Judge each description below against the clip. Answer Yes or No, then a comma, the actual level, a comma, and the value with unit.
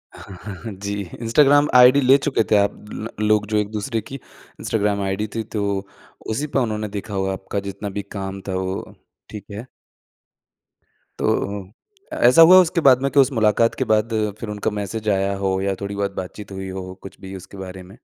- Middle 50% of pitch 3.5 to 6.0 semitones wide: No, average, 2.9 semitones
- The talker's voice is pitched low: Yes, low, 105 Hz